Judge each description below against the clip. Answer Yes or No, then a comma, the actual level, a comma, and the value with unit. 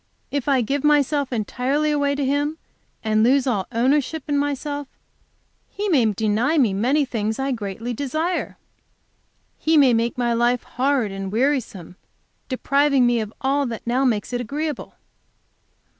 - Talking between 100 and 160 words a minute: Yes, average, 150 wpm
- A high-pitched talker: Yes, very high, 260 Hz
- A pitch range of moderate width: Yes, average, 3.8 semitones